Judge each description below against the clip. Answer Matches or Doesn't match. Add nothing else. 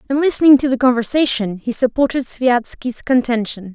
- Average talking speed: Matches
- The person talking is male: Doesn't match